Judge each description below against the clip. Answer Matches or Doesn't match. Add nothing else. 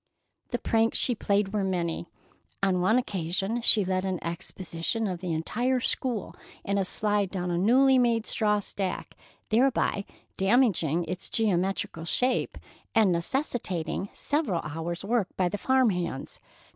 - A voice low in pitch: Doesn't match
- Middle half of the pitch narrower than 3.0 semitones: Doesn't match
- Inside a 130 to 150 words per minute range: Matches